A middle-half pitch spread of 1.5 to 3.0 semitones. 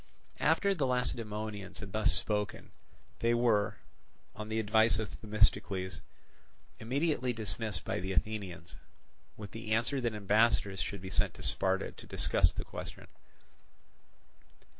Yes: narrow, 2.5 semitones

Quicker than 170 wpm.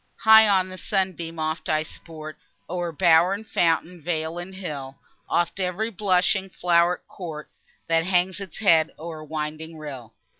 No: average, 150 wpm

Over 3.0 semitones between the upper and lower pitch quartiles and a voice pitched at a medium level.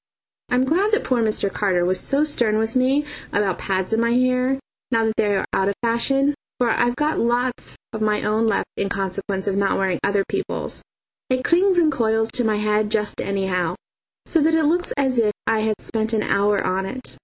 No: average, 4.1 semitones; high, 225 Hz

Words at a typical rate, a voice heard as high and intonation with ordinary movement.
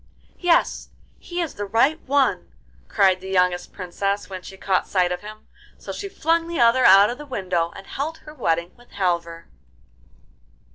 No: average, 175 wpm; high, 200 Hz; wide, 7.4 semitones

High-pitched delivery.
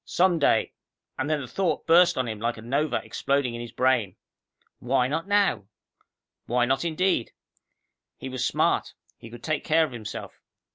No: low, 135 Hz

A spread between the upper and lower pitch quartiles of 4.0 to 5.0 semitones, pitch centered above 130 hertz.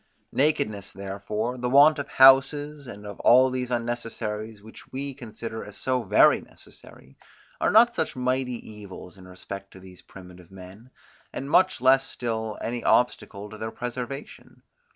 No: average, 4.3 semitones; low, 120 Hz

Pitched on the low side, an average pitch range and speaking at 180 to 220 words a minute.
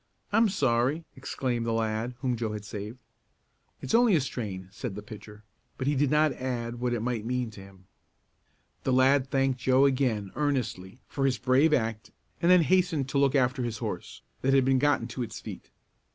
Yes: low, 125 Hz; average, 3.5 semitones; average, 195 wpm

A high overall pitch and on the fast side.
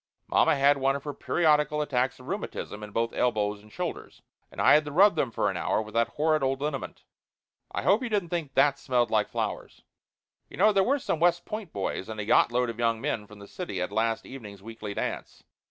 No: low, 135 Hz; fast, 230 wpm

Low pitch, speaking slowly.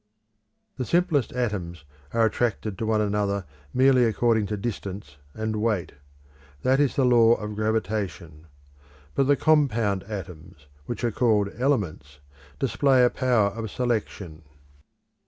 Yes: low, 110 Hz; slow, 130 wpm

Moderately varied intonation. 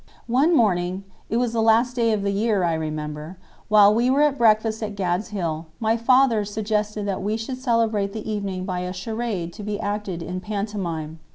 Yes: average, 3.6 semitones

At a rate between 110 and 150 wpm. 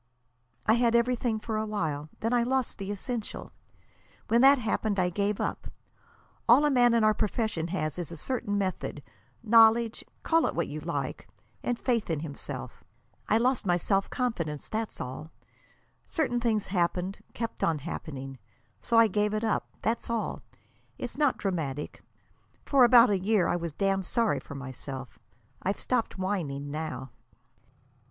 No: average, 160 wpm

